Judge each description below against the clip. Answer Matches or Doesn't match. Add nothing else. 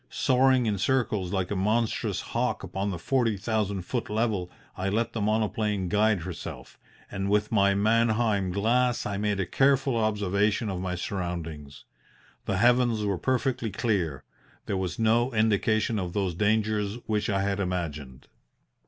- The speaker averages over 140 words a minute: Matches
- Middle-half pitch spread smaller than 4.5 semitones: Matches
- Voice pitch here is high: Doesn't match